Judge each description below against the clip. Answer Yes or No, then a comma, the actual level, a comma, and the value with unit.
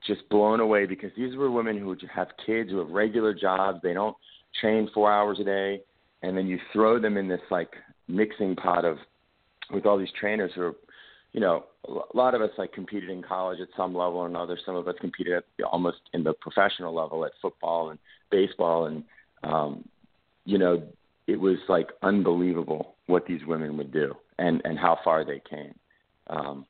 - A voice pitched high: No, very low, 95 Hz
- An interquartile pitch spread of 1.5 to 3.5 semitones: Yes, average, 2.9 semitones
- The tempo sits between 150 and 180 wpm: No, average, 195 wpm